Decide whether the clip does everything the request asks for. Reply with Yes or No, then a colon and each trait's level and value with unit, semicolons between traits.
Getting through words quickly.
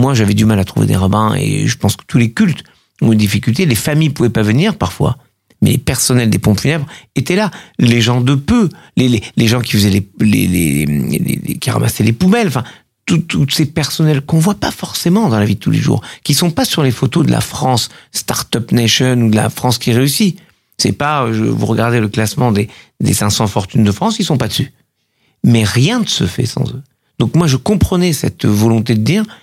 Yes: fast, 245 wpm